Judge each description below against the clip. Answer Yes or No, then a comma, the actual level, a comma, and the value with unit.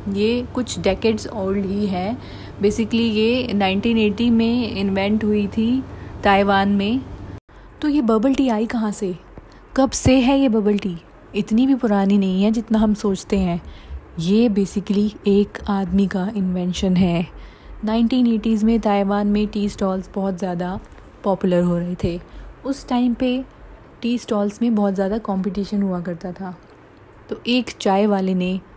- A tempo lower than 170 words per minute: Yes, average, 150 wpm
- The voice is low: No, high, 205 Hz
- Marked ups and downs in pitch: No, average, 2.9 semitones